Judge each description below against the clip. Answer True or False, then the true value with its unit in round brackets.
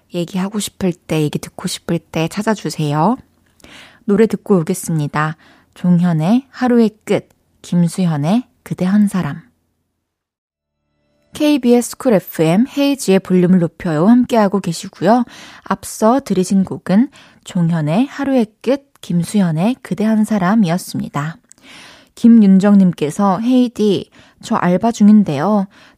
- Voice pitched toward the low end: False (190 Hz)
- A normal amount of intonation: True (4.8 semitones)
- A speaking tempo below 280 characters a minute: True (270 characters per minute)